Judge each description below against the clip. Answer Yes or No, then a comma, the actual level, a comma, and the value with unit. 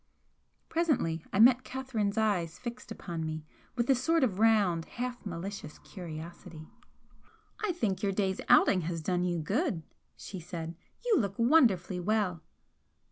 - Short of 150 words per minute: Yes, average, 140 wpm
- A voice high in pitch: Yes, high, 195 Hz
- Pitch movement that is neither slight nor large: No, wide, 5.8 semitones